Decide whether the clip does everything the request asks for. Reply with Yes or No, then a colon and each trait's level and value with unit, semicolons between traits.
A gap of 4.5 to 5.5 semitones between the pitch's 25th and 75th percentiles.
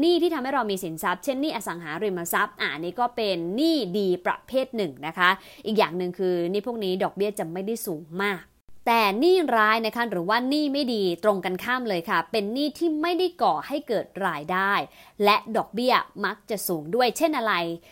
Yes: average, 5.2 semitones